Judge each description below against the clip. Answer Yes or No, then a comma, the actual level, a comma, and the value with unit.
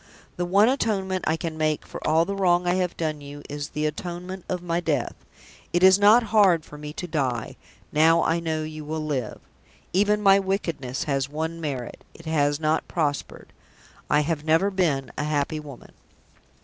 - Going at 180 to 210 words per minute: Yes, average, 185 wpm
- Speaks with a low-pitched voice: No, medium, 160 Hz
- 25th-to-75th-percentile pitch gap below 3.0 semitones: No, average, 3.6 semitones